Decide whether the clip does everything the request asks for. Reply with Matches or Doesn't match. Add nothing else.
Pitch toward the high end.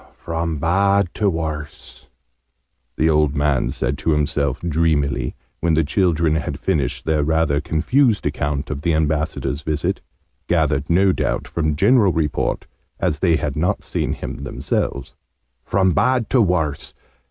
Doesn't match